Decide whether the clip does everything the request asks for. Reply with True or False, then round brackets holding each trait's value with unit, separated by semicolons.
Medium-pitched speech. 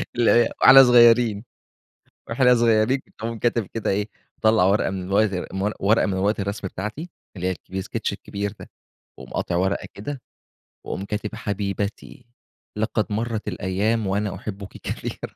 False (105 Hz)